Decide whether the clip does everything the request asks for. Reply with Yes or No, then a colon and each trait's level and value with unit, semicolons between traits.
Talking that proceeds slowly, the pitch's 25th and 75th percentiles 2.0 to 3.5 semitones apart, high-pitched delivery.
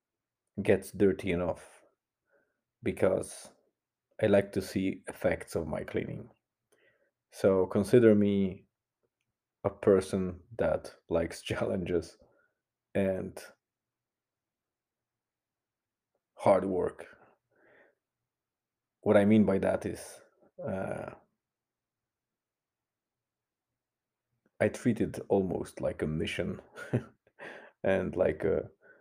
No: slow, 85 wpm; narrow, 2.4 semitones; low, 100 Hz